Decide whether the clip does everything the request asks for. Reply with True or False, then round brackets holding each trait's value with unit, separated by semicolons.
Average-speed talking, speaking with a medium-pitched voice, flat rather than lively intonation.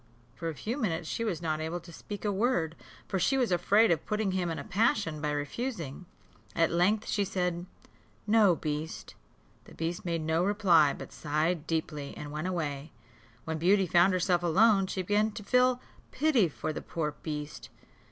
False (180 wpm; 175 Hz; 4.4 semitones)